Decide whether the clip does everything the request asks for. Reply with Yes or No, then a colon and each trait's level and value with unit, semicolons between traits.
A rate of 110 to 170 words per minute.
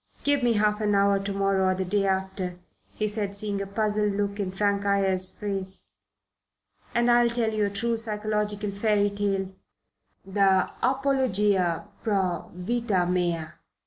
Yes: average, 150 wpm